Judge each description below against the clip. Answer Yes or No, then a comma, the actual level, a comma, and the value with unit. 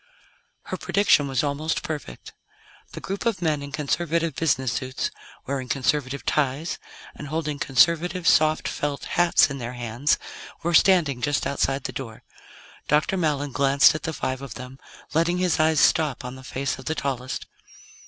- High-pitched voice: No, medium, 145 Hz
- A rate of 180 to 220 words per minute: No, average, 165 wpm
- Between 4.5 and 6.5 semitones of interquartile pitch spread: No, average, 3.3 semitones